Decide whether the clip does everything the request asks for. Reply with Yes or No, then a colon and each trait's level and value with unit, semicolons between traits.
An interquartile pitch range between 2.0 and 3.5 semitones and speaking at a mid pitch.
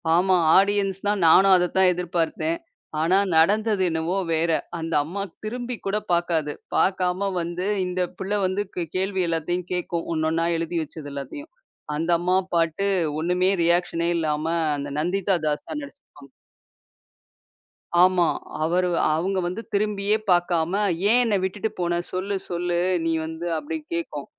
Yes: average, 2.9 semitones; medium, 180 Hz